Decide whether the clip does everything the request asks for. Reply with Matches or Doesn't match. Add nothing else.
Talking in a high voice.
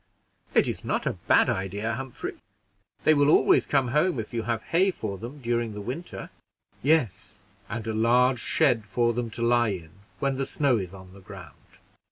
Doesn't match